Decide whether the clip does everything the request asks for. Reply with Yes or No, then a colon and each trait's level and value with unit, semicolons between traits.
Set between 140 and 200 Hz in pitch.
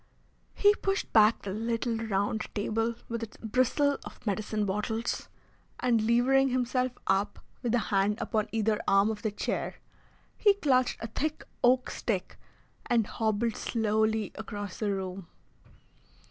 No: high, 225 Hz